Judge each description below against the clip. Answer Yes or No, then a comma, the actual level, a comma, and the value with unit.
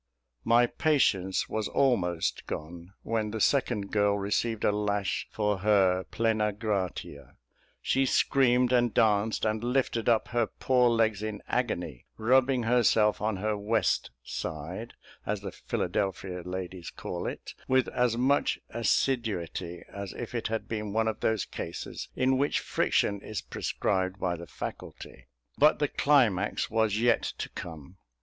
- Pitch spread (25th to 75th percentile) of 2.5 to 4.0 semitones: Yes, average, 3.7 semitones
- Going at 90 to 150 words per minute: Yes, average, 145 wpm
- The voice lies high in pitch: No, low, 110 Hz